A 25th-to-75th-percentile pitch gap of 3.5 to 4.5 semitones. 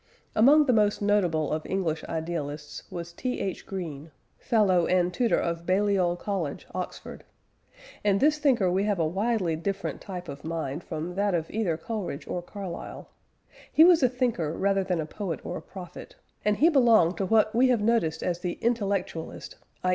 Yes: average, 4.2 semitones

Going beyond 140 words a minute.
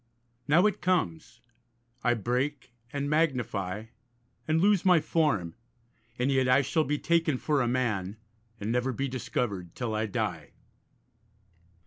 No: slow, 135 wpm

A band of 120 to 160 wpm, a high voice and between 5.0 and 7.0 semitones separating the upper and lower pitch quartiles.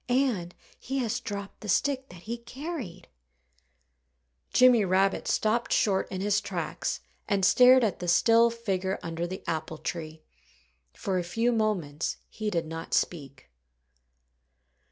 Yes: slow, 135 wpm; high, 200 Hz; average, 5.3 semitones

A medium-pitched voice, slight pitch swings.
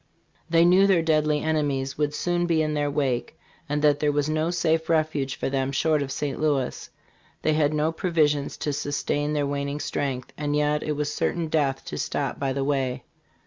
Yes: medium, 150 Hz; narrow, 1.9 semitones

